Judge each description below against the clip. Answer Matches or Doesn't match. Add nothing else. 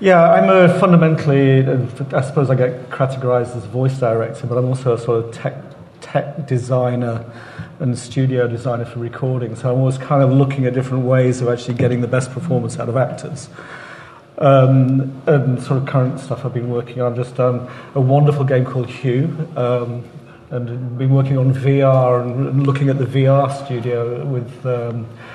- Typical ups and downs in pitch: Doesn't match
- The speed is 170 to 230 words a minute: Matches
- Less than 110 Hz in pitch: Doesn't match